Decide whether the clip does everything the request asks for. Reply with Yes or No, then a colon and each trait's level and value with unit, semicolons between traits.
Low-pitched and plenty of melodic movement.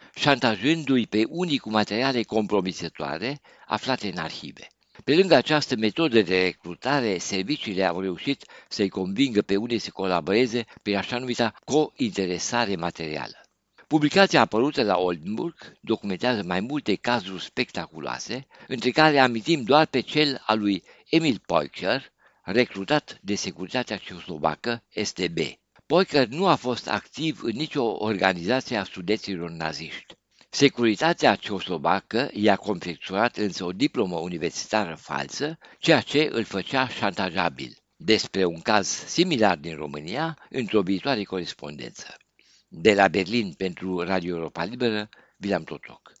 Yes: low, 110 Hz; wide, 6.1 semitones